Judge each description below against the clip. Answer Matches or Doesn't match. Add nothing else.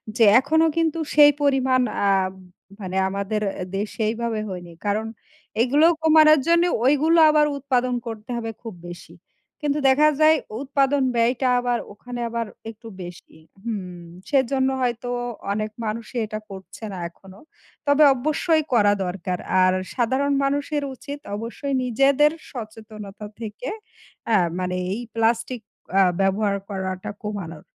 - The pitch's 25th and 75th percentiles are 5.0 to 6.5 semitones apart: Matches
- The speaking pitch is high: Matches